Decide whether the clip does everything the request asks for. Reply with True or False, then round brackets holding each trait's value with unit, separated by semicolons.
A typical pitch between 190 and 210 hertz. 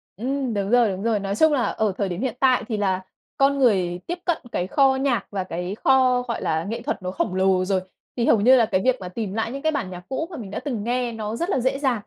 False (230 Hz)